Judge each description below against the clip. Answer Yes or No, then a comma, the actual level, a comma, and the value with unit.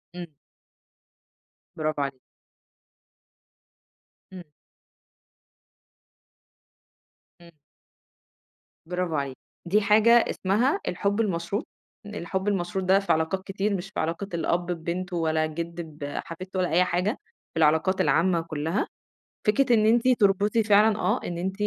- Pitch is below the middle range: No, medium, 180 Hz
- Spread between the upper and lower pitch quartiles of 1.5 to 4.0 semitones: Yes, average, 3.3 semitones